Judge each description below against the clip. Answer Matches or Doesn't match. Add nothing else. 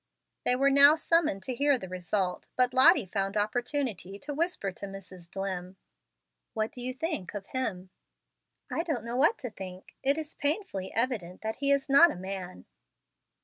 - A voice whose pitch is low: Doesn't match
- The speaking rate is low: Doesn't match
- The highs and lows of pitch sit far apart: Matches